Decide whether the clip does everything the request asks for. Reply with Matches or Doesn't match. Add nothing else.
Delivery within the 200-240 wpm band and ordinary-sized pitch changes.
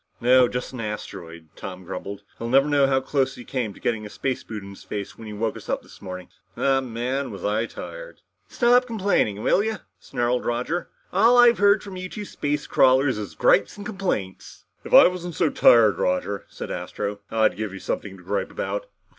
Doesn't match